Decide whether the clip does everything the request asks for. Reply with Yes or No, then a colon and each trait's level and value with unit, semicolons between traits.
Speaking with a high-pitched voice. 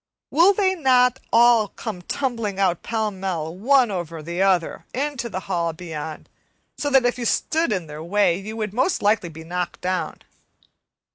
Yes: high, 205 Hz